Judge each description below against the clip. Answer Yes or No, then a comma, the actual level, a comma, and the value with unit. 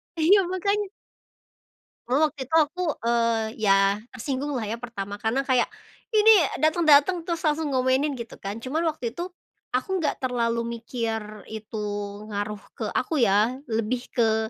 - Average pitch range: No, wide, 5.9 semitones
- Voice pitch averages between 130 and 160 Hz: No, very high, 250 Hz